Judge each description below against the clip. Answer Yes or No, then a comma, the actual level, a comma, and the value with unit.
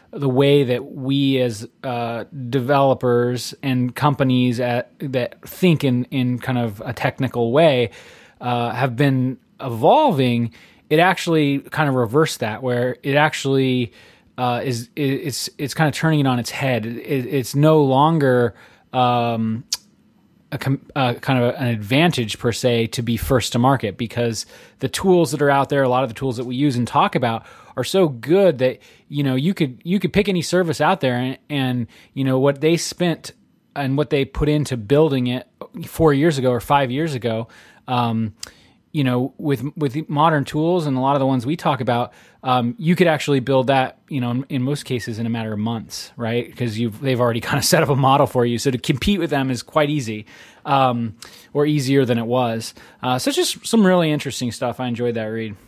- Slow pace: No, average, 200 wpm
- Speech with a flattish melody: No, average, 3.3 semitones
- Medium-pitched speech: No, low, 130 Hz